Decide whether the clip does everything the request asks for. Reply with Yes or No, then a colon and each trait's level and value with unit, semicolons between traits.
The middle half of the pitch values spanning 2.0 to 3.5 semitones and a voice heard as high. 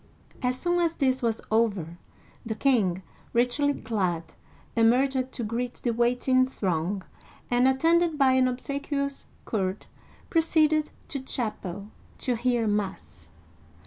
No: average, 4.3 semitones; high, 245 Hz